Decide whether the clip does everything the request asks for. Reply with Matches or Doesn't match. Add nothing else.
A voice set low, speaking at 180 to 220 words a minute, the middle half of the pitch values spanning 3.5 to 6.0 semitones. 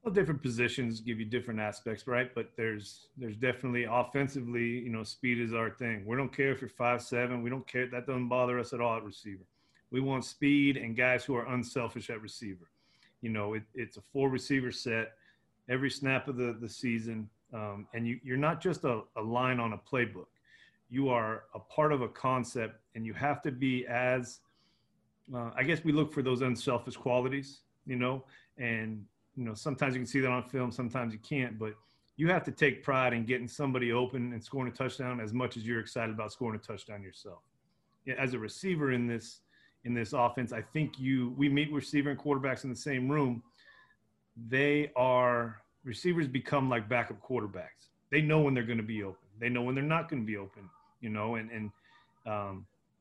Doesn't match